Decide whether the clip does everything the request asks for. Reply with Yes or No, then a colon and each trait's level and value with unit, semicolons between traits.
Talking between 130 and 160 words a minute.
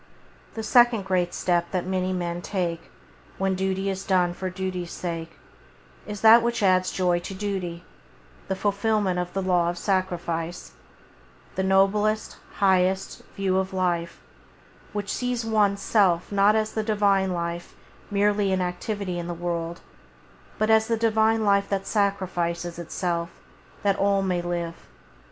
Yes: average, 150 wpm